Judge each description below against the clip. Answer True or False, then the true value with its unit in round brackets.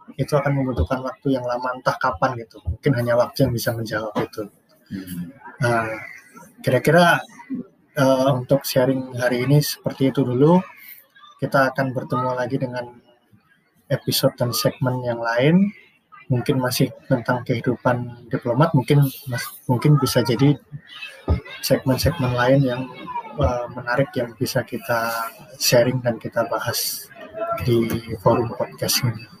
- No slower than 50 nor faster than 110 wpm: False (125 wpm)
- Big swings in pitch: False (2.4 semitones)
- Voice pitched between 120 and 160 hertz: True (130 Hz)